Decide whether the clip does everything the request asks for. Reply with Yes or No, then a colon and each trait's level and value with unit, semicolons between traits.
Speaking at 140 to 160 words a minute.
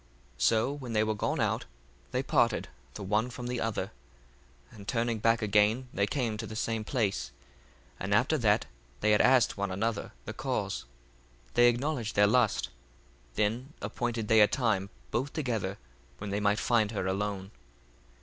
No: average, 170 wpm